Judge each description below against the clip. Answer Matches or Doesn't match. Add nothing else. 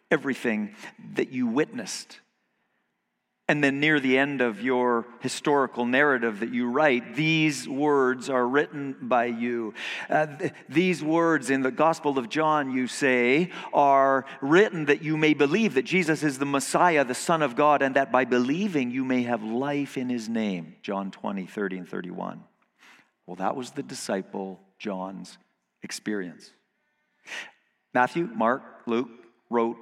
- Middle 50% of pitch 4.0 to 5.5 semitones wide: Matches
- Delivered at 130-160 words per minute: Matches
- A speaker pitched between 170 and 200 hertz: Doesn't match